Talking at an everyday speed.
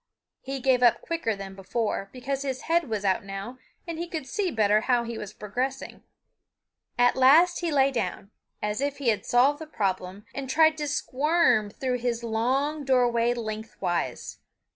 Yes: average, 170 wpm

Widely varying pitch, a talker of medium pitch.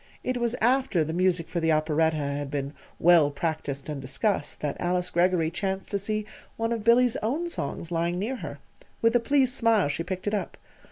Yes: wide, 6.3 semitones; medium, 180 Hz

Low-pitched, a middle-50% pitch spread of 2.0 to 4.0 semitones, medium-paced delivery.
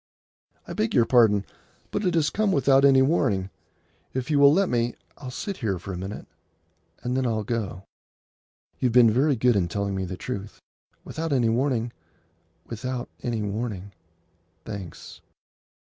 No: low, 120 Hz; average, 4.7 semitones; average, 160 wpm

